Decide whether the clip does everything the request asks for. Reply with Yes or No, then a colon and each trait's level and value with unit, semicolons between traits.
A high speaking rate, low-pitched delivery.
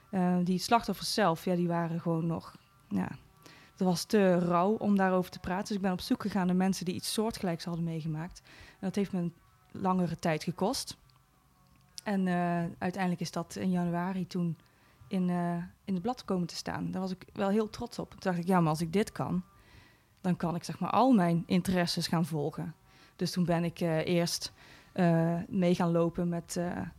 No: fast, 205 wpm; medium, 180 Hz